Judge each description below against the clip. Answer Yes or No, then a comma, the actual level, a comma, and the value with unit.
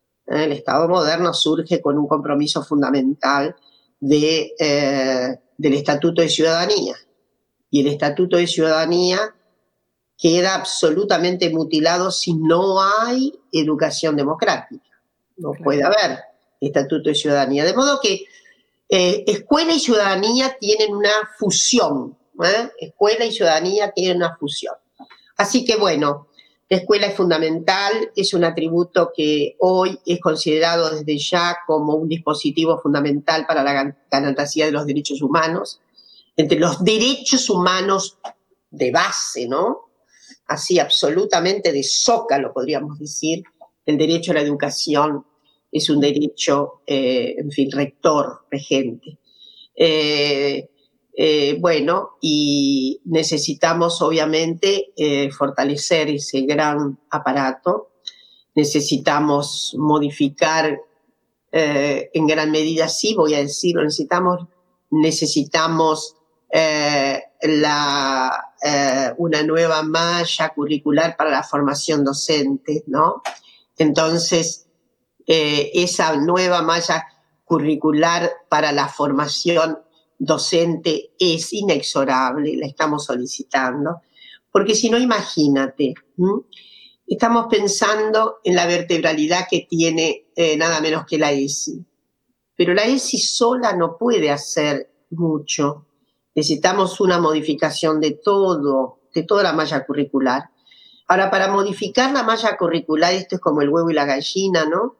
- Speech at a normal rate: No, slow, 120 wpm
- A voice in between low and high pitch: Yes, medium, 160 Hz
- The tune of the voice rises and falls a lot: No, average, 3.7 semitones